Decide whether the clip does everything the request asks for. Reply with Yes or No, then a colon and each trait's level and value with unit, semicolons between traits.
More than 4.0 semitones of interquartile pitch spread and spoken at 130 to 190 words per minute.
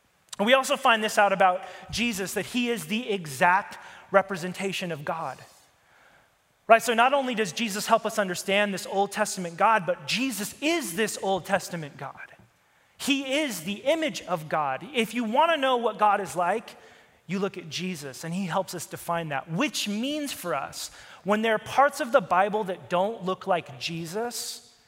Yes: average, 4.5 semitones; average, 185 wpm